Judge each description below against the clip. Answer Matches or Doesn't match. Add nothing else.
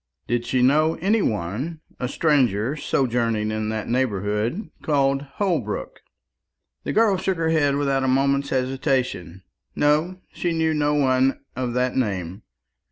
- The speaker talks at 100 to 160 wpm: Matches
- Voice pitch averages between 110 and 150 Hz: Matches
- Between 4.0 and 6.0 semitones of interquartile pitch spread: Matches